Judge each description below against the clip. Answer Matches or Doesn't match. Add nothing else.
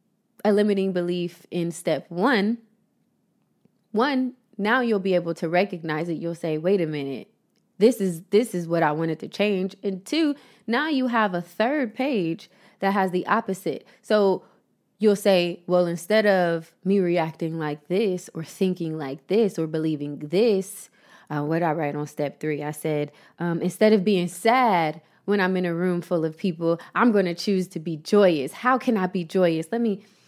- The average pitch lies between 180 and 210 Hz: Matches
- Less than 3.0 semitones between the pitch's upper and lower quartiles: Doesn't match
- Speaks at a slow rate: Doesn't match